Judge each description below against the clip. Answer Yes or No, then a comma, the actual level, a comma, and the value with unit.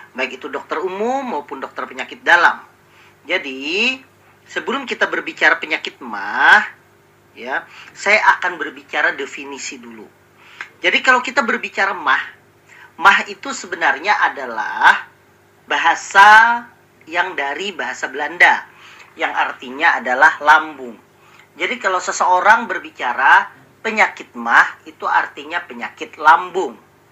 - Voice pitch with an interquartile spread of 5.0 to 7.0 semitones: Yes, wide, 5.5 semitones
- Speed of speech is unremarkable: Yes, average, 105 wpm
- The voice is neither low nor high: No, high, 200 Hz